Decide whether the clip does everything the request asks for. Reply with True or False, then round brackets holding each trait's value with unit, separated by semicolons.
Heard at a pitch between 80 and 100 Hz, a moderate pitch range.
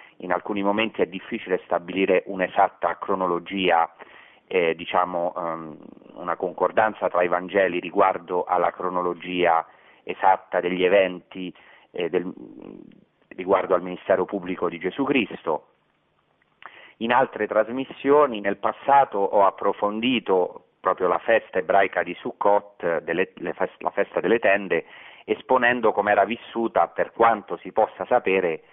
True (95 Hz; 3.4 semitones)